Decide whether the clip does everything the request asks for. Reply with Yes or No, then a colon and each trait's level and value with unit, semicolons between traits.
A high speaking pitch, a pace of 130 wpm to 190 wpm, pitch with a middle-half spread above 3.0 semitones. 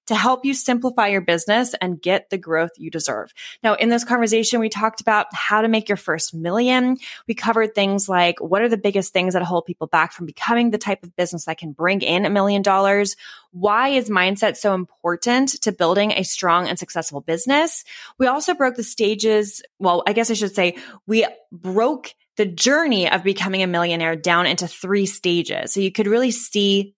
No: high, 200 Hz; average, 200 wpm; average, 4.4 semitones